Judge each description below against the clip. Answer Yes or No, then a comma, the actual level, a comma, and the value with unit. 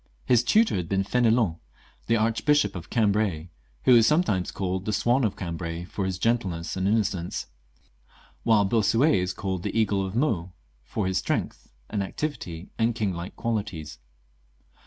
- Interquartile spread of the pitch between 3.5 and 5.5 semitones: Yes, average, 3.9 semitones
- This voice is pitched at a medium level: No, low, 100 Hz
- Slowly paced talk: No, average, 160 wpm